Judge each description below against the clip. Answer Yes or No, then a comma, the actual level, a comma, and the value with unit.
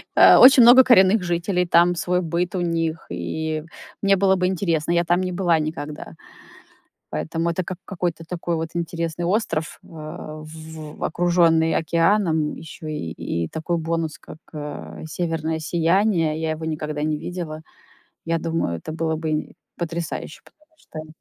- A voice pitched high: No, medium, 165 Hz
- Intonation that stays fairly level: Yes, narrow, 2.1 semitones